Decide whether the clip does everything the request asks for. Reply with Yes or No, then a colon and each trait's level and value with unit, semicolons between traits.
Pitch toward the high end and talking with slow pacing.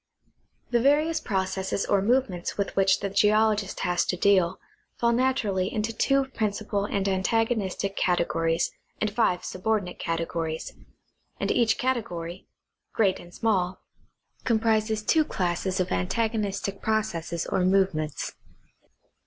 Yes: high, 200 Hz; slow, 120 wpm